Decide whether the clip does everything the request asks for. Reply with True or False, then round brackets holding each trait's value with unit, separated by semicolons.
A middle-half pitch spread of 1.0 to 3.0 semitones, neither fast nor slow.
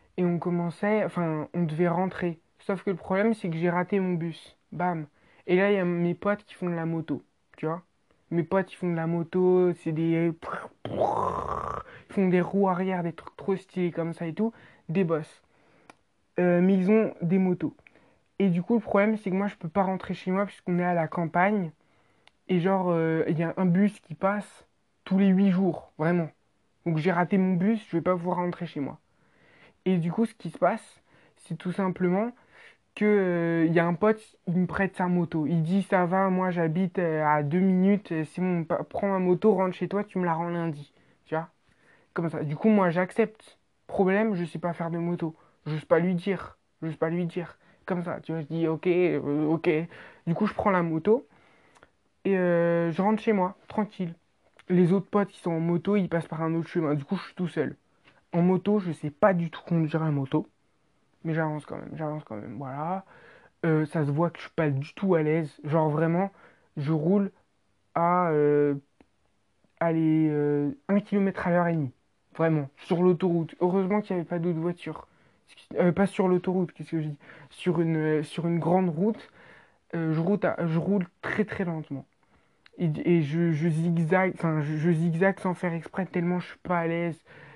True (2.7 semitones; 210 wpm)